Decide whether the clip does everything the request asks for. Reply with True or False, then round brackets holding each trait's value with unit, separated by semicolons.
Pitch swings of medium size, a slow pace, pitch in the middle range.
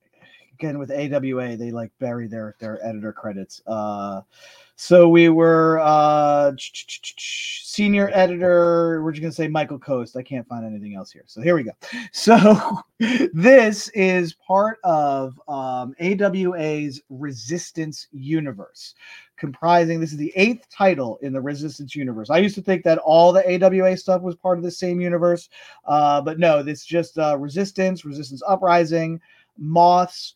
False (4.7 semitones; 155 wpm; 165 Hz)